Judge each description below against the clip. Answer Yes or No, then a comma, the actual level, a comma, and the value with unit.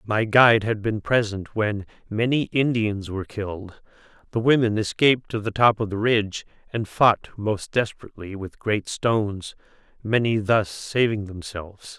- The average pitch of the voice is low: Yes, low, 105 Hz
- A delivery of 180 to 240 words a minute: No, average, 150 wpm